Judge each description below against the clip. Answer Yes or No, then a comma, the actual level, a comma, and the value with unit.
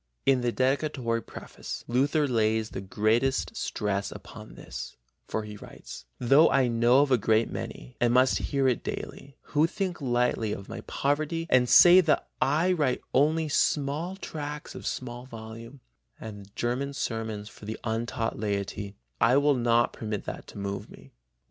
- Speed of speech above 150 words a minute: Yes, average, 165 wpm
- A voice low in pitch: Yes, low, 125 Hz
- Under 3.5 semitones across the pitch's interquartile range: No, average, 4.2 semitones